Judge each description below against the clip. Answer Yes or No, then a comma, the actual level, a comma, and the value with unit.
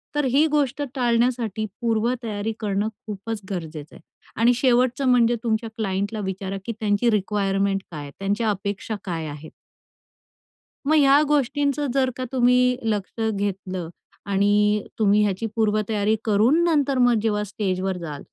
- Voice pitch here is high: Yes, high, 215 Hz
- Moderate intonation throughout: Yes, average, 3.8 semitones